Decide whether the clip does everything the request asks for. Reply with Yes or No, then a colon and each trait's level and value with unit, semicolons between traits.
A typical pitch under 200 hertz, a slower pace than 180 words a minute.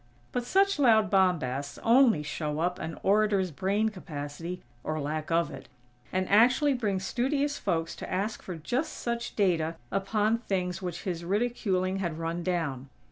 Yes: medium, 185 Hz; average, 155 wpm